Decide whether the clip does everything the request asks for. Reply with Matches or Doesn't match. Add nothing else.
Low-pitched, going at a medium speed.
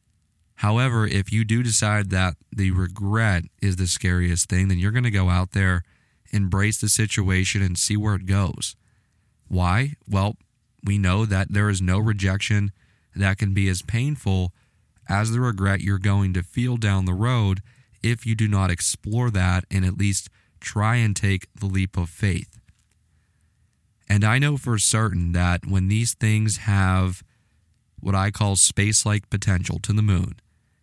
Matches